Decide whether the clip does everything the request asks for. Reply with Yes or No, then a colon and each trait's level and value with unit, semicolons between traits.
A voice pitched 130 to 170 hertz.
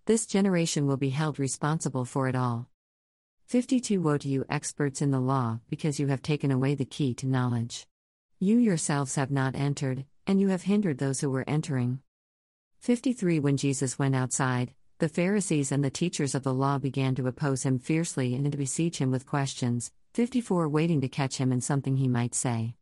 Yes: medium, 140 Hz